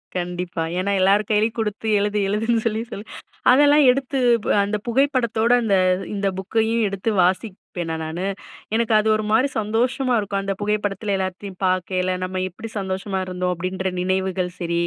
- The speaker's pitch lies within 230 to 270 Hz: No, high, 200 Hz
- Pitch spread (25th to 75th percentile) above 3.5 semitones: No, average, 3.2 semitones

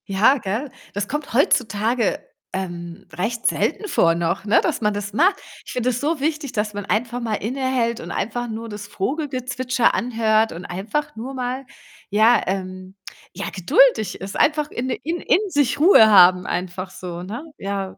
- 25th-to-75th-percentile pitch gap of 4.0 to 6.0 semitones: Yes, average, 4.9 semitones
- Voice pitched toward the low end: No, high, 220 Hz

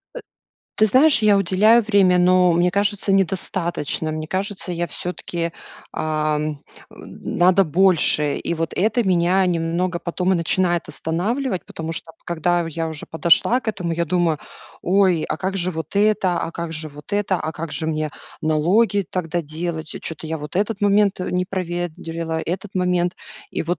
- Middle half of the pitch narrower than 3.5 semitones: Yes, average, 2.9 semitones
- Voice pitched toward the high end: No, medium, 175 Hz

